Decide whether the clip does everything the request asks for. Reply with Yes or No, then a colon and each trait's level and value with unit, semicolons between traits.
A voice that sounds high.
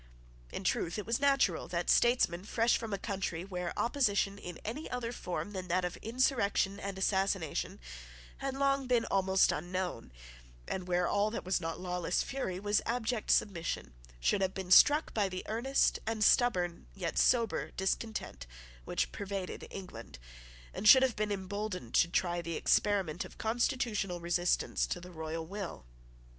Yes: high, 195 Hz